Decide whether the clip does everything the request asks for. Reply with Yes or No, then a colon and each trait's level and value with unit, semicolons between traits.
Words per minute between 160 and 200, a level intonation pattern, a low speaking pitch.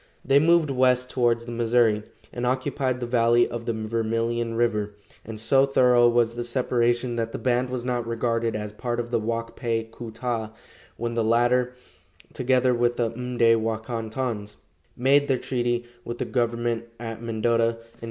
Yes: average, 180 wpm; narrow, 1.5 semitones; low, 120 Hz